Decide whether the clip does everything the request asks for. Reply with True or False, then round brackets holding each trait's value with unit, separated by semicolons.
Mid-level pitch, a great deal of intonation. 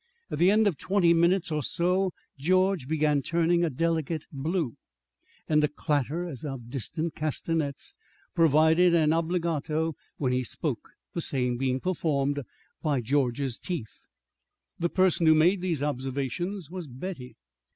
False (160 Hz; 3.8 semitones)